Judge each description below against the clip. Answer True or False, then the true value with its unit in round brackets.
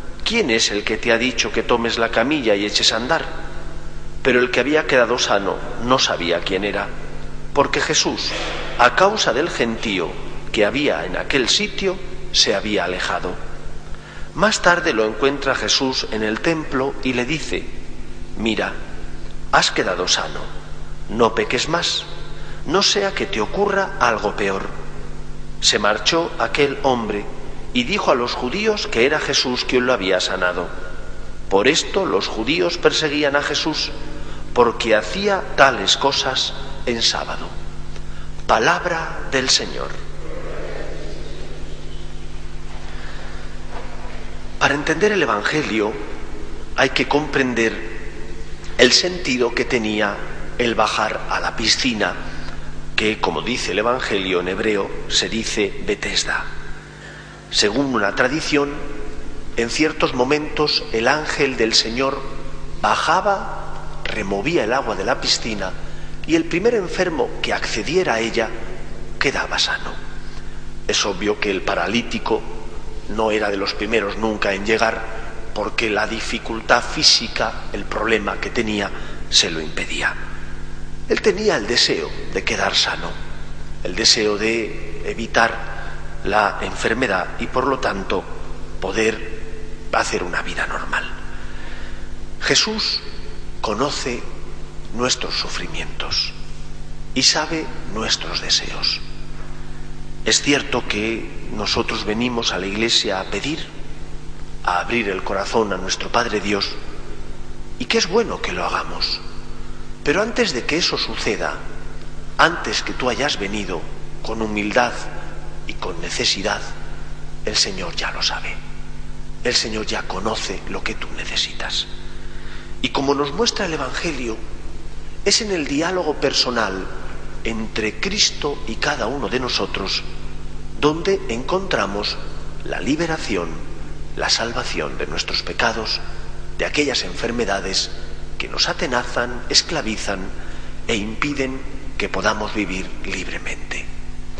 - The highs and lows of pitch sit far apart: True (6.2 semitones)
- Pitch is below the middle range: True (115 Hz)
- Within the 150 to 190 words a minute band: False (125 wpm)